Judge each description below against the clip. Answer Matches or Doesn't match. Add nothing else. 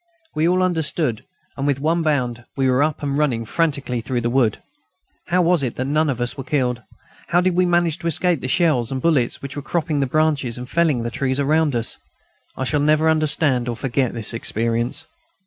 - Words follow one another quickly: Matches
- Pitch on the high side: Doesn't match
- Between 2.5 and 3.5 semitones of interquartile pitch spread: Doesn't match